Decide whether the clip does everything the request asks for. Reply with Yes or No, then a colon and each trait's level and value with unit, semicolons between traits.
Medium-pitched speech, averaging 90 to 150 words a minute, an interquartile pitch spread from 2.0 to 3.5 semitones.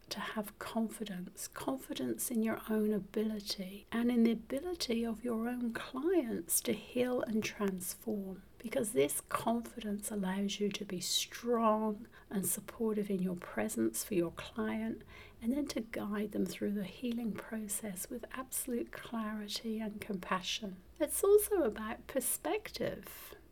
No: high, 220 Hz; average, 140 wpm; average, 2.7 semitones